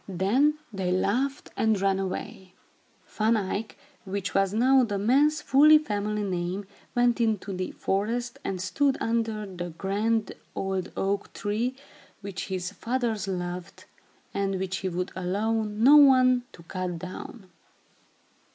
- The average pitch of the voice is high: Yes, high, 205 Hz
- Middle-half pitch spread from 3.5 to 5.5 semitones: Yes, average, 3.8 semitones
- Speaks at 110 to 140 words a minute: Yes, slow, 135 wpm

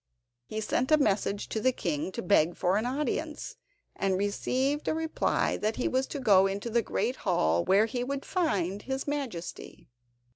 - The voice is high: Yes, high, 220 Hz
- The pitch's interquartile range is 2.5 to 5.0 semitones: No, wide, 5.5 semitones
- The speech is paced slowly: No, average, 180 wpm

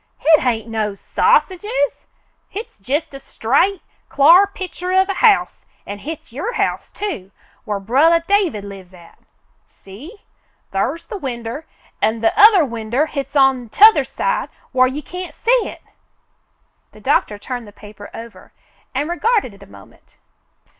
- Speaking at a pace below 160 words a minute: Yes, average, 145 wpm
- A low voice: No, very high, 275 Hz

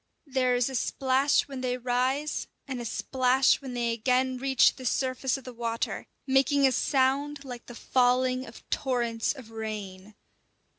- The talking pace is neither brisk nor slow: Yes, average, 160 wpm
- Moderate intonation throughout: No, narrow, 1.8 semitones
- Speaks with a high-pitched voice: Yes, very high, 255 Hz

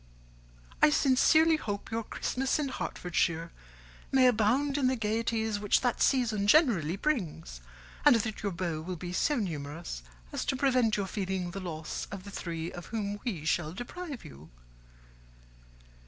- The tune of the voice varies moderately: No, wide, 6.5 semitones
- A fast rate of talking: No, average, 155 wpm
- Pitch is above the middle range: Yes, high, 205 Hz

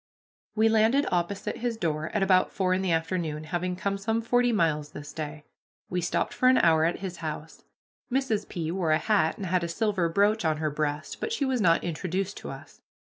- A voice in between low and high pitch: Yes, medium, 180 Hz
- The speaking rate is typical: No, fast, 210 wpm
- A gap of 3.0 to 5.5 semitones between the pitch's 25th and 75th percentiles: Yes, average, 4.9 semitones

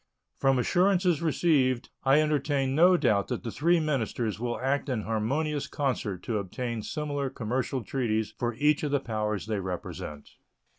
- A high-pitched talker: No, low, 130 Hz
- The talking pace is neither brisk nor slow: Yes, average, 155 wpm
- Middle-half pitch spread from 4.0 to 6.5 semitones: Yes, average, 5.1 semitones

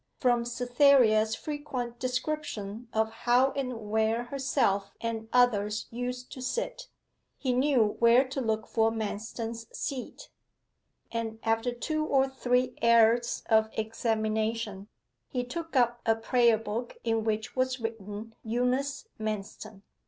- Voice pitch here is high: Yes, high, 235 Hz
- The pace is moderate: No, slow, 125 wpm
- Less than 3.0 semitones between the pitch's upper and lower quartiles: Yes, narrow, 2.4 semitones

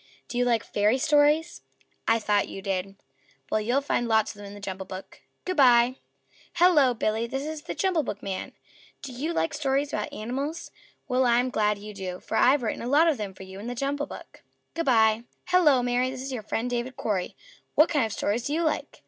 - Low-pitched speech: No, high, 245 Hz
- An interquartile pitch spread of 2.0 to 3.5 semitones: No, average, 5.1 semitones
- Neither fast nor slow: No, fast, 215 wpm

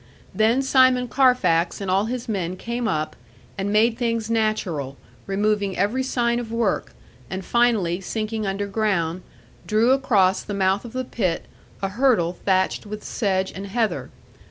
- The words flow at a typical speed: Yes, average, 150 wpm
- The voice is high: Yes, high, 215 Hz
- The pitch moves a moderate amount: Yes, average, 3.7 semitones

